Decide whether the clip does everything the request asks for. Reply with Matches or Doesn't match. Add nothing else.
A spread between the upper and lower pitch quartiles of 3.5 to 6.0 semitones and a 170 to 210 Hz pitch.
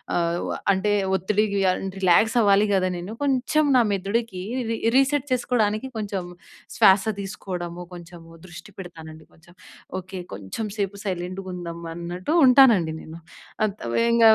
Matches